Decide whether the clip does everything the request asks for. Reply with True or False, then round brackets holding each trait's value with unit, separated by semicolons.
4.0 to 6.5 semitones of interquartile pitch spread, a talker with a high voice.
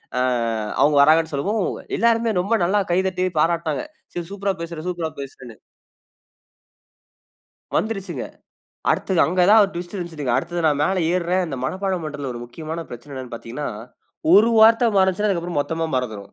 False (4.4 semitones; 170 Hz)